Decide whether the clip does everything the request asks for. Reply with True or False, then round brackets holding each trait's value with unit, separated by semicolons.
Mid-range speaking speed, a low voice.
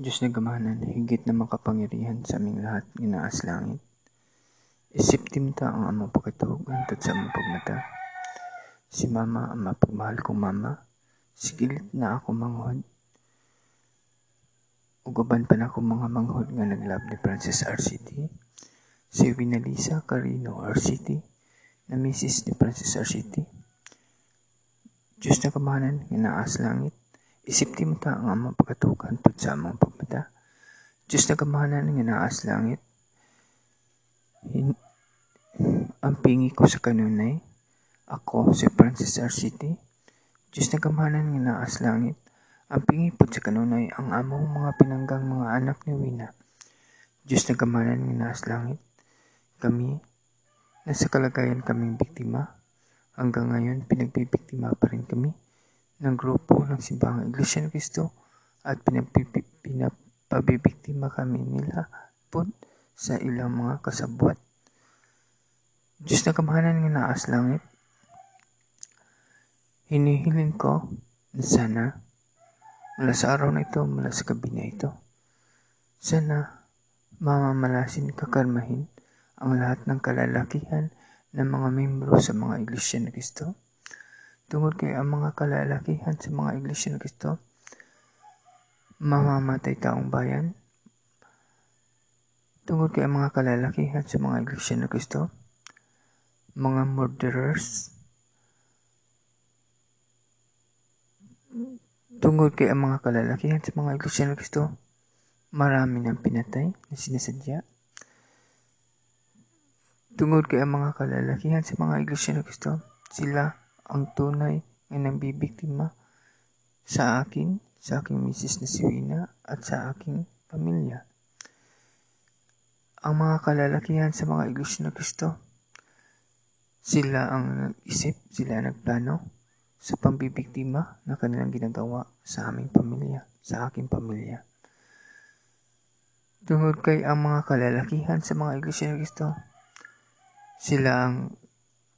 False (120 wpm; 130 Hz)